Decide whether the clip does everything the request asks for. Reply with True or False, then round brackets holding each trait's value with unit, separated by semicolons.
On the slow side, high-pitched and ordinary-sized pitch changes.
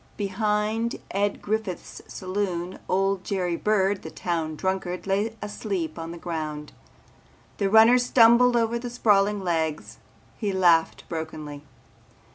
True (120 wpm; 195 Hz; 4.0 semitones)